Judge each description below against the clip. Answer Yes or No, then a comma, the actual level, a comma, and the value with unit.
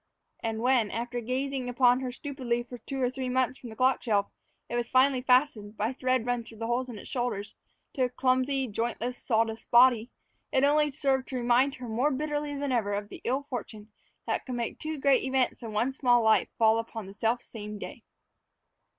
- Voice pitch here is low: No, high, 245 Hz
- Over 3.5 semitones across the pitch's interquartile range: No, narrow, 2.6 semitones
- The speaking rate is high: Yes, fast, 210 wpm